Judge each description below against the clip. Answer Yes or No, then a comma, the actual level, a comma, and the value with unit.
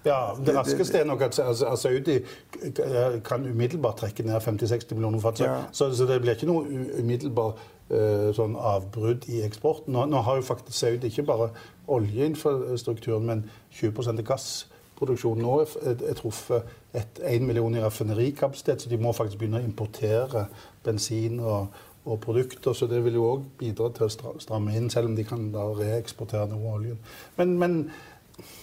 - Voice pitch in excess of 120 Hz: No, low, 115 Hz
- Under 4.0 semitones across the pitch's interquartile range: Yes, narrow, 2.5 semitones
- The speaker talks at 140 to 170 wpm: Yes, average, 155 wpm